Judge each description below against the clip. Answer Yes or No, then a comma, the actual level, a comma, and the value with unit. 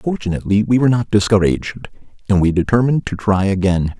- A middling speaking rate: Yes, average, 165 wpm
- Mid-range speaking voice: No, low, 105 Hz